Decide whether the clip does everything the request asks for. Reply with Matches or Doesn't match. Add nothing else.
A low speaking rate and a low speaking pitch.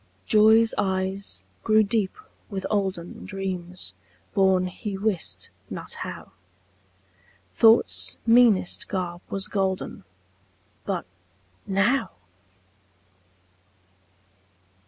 Doesn't match